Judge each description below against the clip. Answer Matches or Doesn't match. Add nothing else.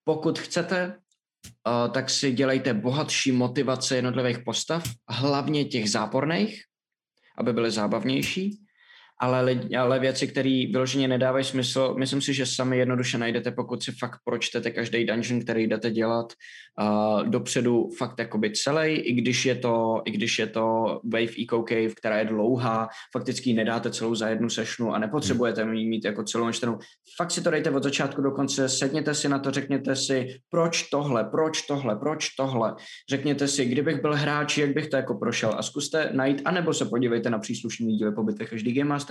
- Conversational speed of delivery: Doesn't match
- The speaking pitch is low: Matches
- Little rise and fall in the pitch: Doesn't match